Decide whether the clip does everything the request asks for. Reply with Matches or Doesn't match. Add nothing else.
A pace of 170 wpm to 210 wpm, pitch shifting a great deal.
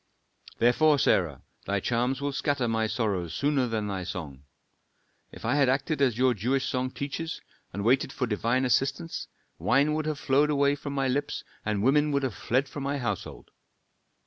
Doesn't match